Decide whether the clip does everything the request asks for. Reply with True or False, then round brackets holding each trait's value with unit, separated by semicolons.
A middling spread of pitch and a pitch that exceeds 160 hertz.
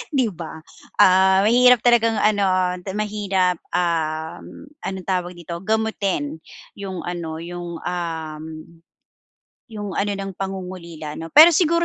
True (3.5 semitones; 185 Hz)